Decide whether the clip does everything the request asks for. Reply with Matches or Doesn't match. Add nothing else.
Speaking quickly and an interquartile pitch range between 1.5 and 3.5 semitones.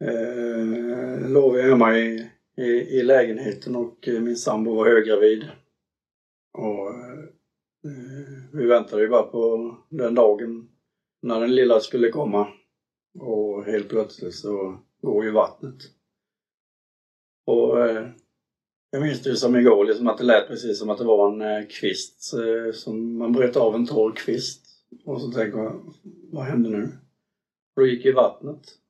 Doesn't match